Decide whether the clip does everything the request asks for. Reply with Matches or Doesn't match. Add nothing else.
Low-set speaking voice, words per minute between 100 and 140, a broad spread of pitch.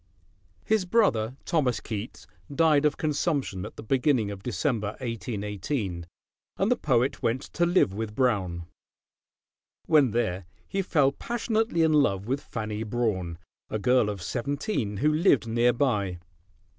Matches